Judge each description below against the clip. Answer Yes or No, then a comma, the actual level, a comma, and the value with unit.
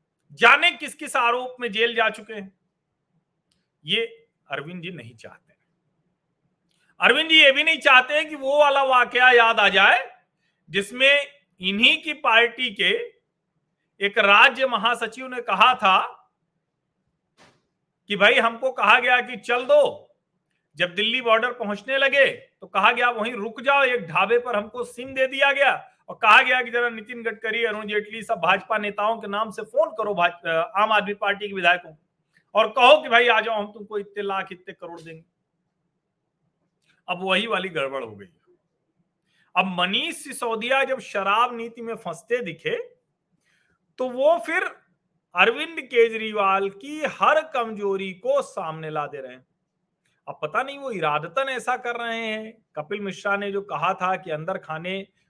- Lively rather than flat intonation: Yes, wide, 5.8 semitones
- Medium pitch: No, high, 210 Hz